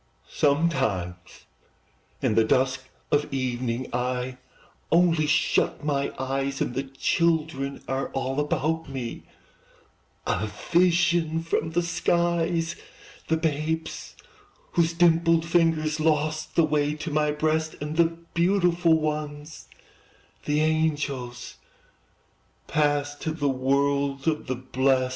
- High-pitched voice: No, medium, 150 Hz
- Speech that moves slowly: Yes, slow, 110 wpm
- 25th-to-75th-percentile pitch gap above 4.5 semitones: No, average, 3.3 semitones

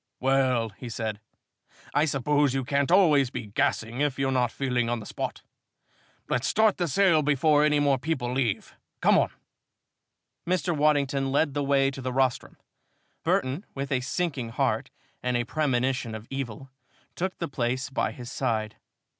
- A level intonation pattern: No, average, 3.0 semitones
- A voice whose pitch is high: No, low, 135 Hz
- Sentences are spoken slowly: No, average, 165 wpm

